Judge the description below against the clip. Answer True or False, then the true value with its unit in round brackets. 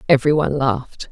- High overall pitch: False (135 Hz)